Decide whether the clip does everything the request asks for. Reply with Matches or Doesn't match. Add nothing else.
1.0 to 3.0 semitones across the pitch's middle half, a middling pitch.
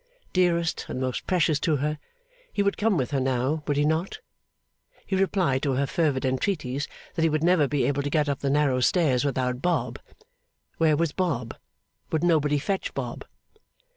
Doesn't match